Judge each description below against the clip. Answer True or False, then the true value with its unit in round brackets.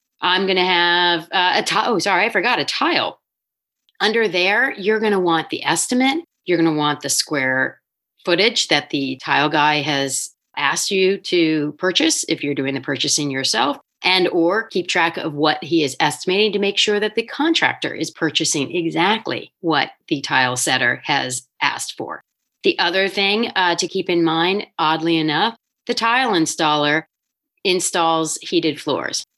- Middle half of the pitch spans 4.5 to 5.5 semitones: True (4.9 semitones)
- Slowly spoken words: False (170 wpm)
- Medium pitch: True (170 Hz)